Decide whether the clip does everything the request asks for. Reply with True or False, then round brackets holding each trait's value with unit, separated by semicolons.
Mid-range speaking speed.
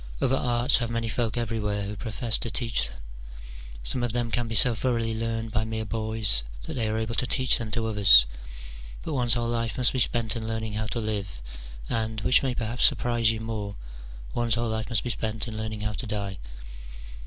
False (210 wpm)